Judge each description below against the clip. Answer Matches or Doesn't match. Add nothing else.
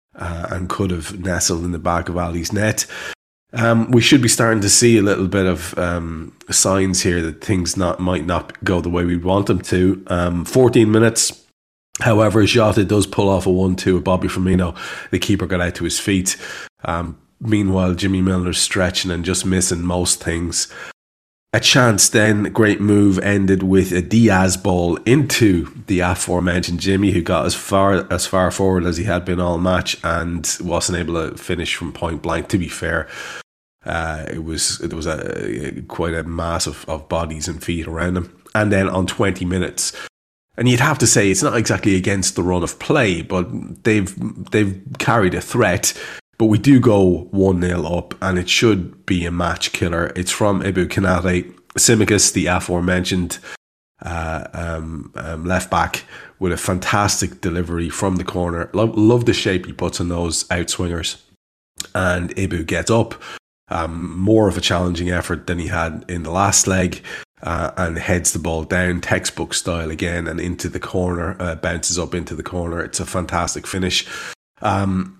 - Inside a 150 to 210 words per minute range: Matches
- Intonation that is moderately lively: Doesn't match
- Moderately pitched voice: Doesn't match